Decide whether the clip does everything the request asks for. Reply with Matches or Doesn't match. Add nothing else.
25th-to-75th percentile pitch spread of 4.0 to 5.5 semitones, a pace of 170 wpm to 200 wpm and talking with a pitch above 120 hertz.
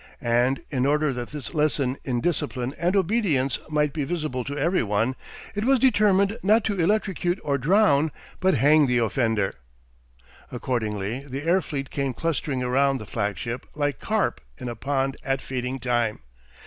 Doesn't match